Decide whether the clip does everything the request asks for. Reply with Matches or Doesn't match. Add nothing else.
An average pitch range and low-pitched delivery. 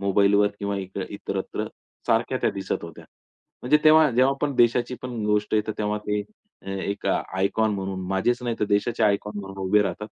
Matches